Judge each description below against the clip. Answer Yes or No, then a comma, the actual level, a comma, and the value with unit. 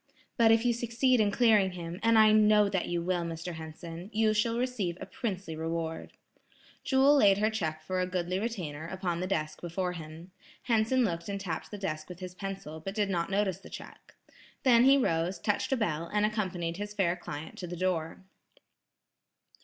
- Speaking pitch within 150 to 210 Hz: Yes, high, 190 Hz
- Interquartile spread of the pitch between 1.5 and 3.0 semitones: No, average, 4.2 semitones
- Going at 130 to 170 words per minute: No, average, 195 wpm